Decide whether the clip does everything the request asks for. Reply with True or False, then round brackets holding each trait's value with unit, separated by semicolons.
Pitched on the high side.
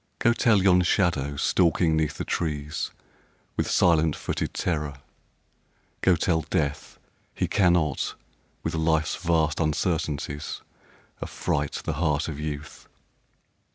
False (80 Hz)